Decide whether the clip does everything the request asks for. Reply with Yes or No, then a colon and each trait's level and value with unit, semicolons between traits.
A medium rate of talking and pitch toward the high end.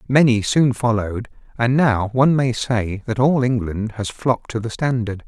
No: average, 180 wpm; low, 120 Hz